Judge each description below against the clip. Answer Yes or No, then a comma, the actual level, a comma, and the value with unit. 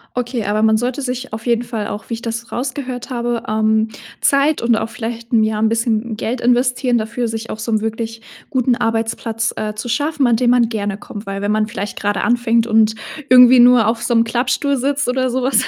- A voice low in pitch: No, high, 230 Hz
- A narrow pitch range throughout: Yes, narrow, 2.0 semitones